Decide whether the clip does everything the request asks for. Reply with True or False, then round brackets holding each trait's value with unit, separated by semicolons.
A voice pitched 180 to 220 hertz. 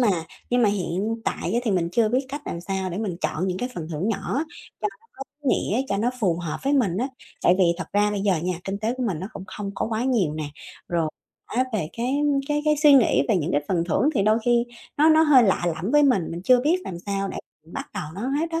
True (210 Hz)